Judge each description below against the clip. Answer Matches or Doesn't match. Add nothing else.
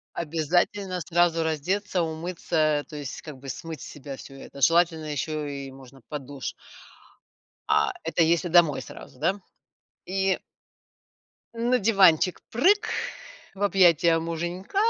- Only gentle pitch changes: Doesn't match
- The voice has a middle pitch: Matches